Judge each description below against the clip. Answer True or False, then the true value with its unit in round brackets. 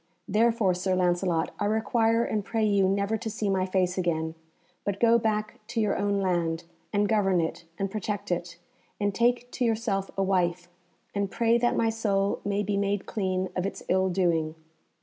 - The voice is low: False (200 Hz)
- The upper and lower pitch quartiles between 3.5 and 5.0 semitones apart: False (3.0 semitones)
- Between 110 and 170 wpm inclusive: False (185 wpm)